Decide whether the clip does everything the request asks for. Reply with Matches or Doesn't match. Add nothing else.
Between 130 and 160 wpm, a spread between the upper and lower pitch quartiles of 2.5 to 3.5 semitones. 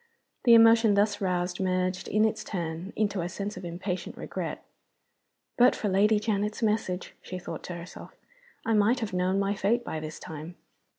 Doesn't match